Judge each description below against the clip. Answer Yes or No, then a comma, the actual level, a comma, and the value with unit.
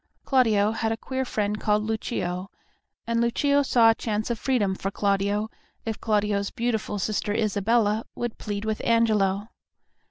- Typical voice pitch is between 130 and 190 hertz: No, high, 215 Hz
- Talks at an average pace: Yes, average, 150 wpm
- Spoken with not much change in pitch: Yes, narrow, 2.1 semitones